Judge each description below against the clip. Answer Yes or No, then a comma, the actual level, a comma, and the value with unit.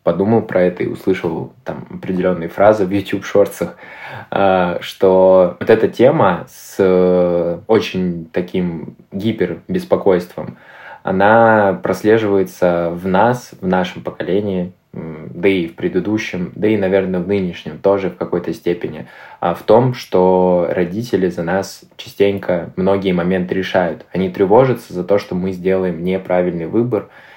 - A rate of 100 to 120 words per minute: No, average, 130 wpm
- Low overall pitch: Yes, very low, 95 Hz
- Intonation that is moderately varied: No, narrow, 1.7 semitones